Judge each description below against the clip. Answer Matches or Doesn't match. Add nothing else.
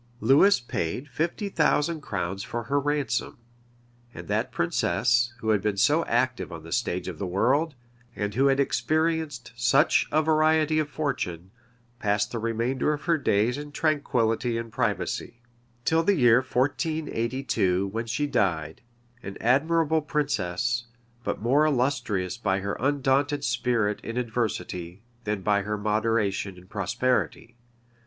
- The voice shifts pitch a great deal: Matches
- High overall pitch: Doesn't match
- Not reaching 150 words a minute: Matches